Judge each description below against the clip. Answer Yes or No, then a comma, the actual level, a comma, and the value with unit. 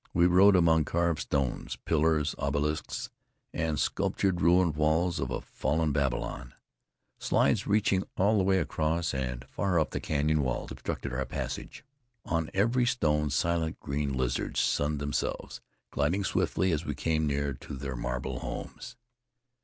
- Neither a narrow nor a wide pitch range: Yes, average, 3.4 semitones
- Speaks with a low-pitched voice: Yes, very low, 75 Hz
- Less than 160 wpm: Yes, average, 145 wpm